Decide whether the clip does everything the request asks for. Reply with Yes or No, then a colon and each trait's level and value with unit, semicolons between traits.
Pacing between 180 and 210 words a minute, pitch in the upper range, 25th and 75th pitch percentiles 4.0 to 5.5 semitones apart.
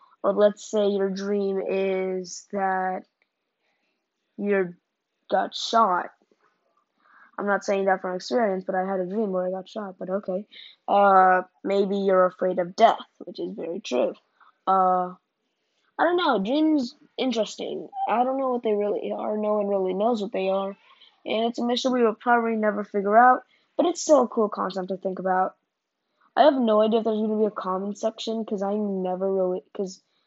No: average, 185 wpm; high, 205 Hz; average, 3.3 semitones